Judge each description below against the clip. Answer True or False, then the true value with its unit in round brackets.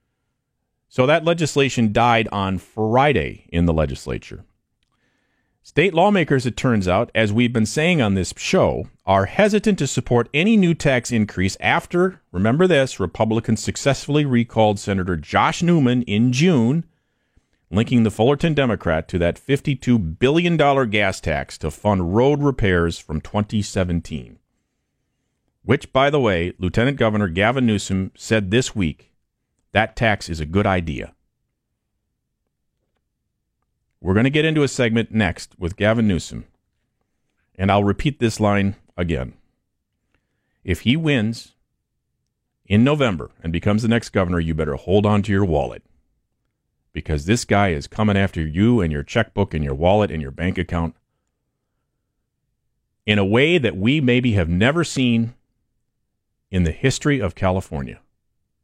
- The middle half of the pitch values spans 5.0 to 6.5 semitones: True (5.6 semitones)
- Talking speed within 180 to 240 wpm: False (140 wpm)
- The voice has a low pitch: True (110 Hz)